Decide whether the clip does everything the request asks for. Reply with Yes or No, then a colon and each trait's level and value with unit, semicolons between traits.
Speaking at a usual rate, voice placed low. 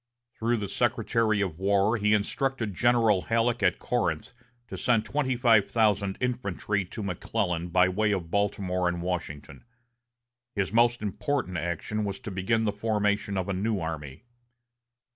Yes: average, 150 wpm; low, 105 Hz